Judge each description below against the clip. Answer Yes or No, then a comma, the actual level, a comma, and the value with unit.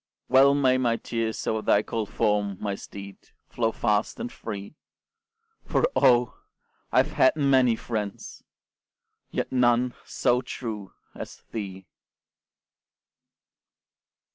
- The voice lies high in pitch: No, low, 115 Hz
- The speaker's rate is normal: No, slow, 115 wpm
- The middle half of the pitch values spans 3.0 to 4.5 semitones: Yes, average, 3.4 semitones